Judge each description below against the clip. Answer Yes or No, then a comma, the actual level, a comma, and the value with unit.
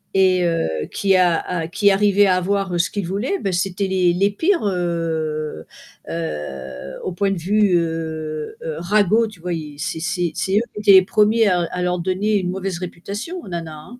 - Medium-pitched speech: Yes, medium, 180 Hz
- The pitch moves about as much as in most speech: Yes, average, 3.3 semitones